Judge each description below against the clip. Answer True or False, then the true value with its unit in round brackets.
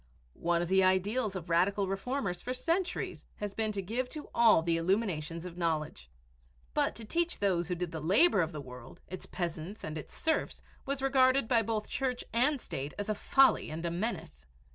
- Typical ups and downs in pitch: False (6.3 semitones)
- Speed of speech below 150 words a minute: False (195 wpm)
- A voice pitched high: True (195 Hz)